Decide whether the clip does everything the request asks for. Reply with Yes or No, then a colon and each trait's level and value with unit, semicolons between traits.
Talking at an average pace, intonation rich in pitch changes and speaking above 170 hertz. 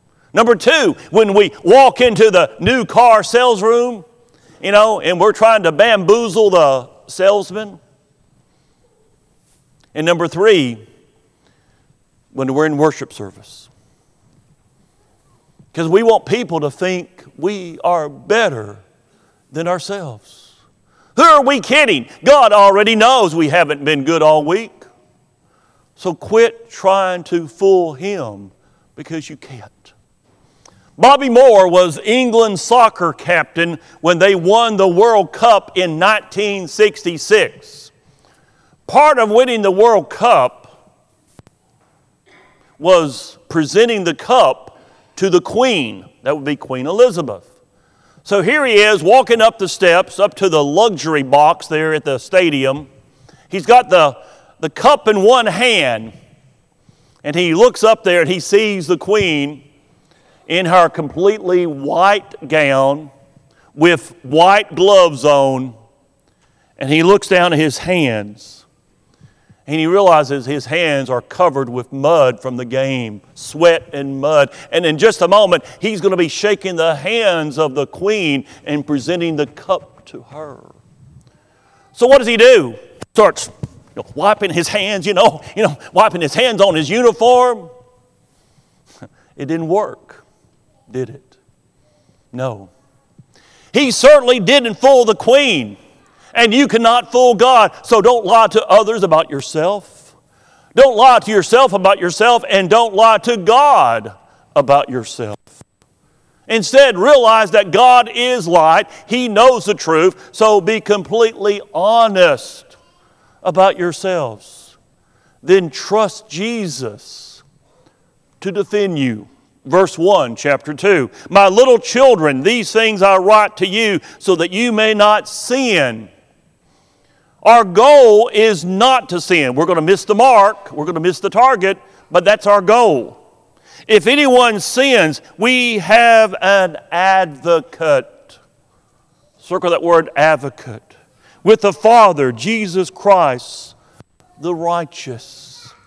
No: slow, 130 wpm; wide, 6.4 semitones; medium, 185 Hz